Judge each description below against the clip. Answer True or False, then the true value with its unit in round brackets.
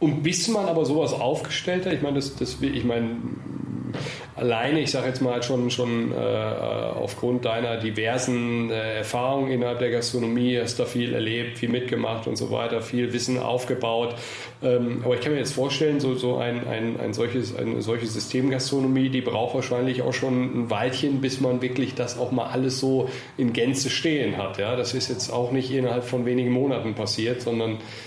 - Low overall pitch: True (125 Hz)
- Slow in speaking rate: False (190 wpm)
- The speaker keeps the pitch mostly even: True (1.9 semitones)